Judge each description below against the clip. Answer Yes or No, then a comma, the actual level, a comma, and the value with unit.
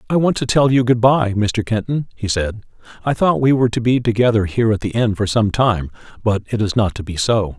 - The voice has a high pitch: No, low, 115 Hz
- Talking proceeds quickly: Yes, fast, 255 wpm